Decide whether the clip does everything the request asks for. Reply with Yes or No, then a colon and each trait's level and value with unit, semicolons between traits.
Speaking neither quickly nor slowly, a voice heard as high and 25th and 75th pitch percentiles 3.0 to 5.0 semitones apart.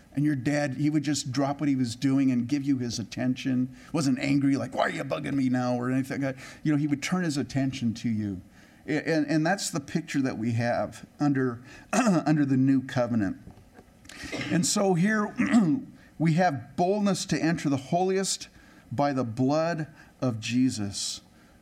No: average, 185 wpm; medium, 140 Hz; average, 3.7 semitones